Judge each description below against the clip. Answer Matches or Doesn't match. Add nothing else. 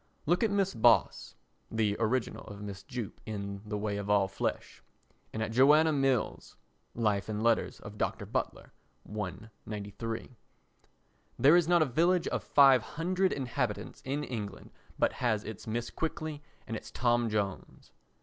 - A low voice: Matches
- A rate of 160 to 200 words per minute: Doesn't match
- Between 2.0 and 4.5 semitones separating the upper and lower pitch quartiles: Doesn't match